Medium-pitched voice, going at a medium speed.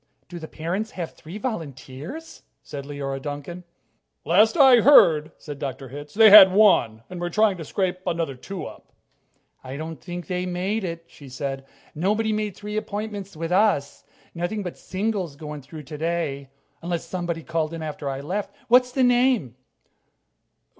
Yes: medium, 170 Hz; average, 160 wpm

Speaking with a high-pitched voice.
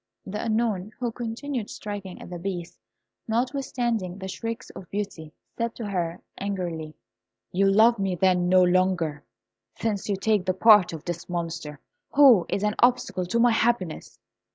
Yes: high, 195 Hz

